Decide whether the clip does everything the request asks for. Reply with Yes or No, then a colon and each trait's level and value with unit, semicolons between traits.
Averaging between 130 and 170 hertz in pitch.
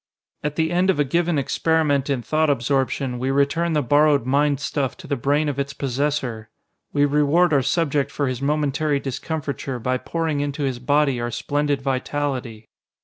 Yes: medium, 140 Hz